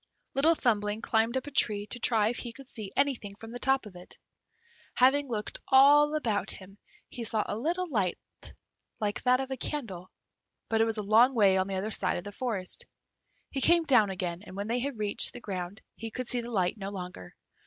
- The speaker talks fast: Yes, fast, 215 wpm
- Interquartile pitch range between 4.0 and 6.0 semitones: Yes, average, 4.3 semitones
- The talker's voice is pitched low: No, high, 225 Hz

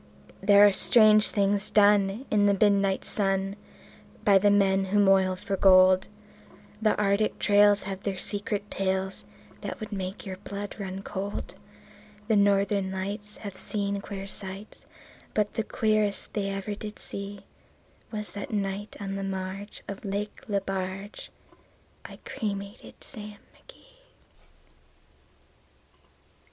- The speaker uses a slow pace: Yes, slow, 130 wpm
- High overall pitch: Yes, high, 200 Hz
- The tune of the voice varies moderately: No, narrow, 1.2 semitones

